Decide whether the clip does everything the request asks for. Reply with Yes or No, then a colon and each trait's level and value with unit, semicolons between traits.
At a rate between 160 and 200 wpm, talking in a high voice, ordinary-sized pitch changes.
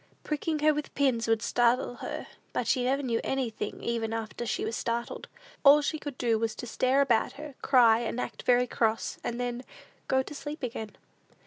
Yes: average, 195 wpm; high, 245 Hz; average, 3.3 semitones